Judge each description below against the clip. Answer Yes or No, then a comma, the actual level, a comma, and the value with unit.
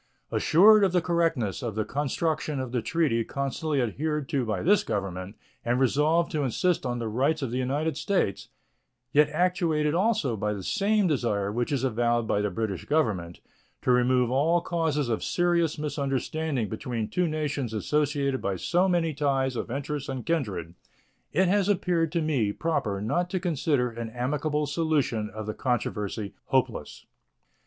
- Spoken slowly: No, average, 165 wpm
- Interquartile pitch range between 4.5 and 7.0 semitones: Yes, wide, 5.5 semitones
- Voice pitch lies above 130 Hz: Yes, medium, 140 Hz